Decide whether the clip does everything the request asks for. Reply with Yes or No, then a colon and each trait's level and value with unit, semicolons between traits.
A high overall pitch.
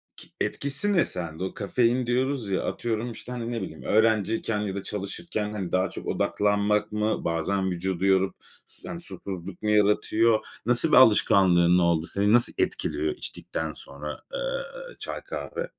No: low, 105 Hz